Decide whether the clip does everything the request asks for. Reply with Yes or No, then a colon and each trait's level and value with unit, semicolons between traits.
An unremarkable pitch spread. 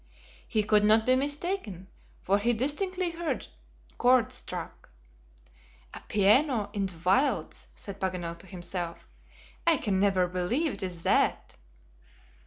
No: wide, 6.2 semitones